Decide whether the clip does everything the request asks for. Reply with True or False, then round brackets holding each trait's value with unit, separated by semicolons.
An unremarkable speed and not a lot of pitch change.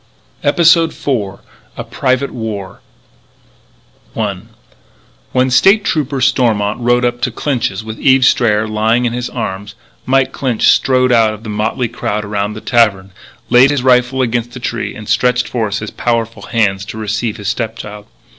False (155 wpm; 3.0 semitones)